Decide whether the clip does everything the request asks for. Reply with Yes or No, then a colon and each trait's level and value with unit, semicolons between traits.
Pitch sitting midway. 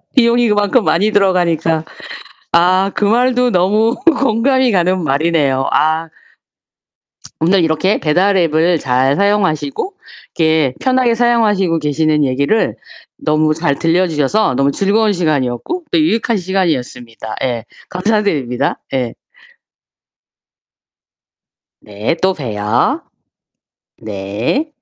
Yes: medium, 170 Hz